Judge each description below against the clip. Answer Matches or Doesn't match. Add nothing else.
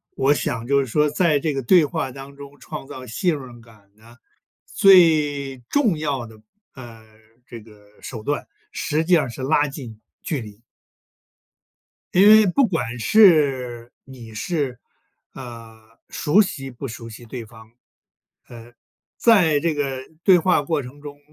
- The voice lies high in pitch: Doesn't match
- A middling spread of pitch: Matches